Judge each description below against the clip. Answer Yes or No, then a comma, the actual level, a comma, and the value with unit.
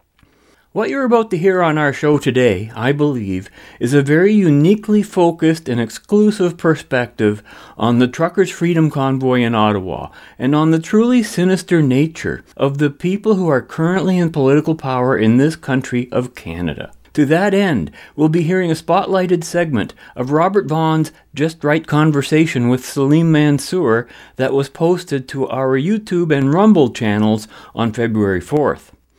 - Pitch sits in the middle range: Yes, medium, 150 Hz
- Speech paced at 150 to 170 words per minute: Yes, average, 155 wpm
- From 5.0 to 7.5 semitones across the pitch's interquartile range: Yes, wide, 5.5 semitones